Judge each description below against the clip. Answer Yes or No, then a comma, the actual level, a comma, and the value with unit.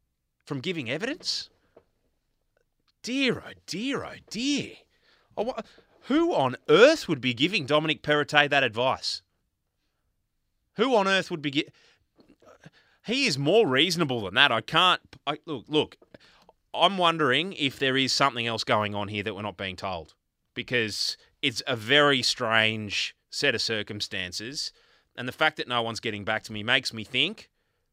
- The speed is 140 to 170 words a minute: Yes, average, 155 wpm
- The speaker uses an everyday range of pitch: No, wide, 6.7 semitones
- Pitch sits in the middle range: No, low, 125 Hz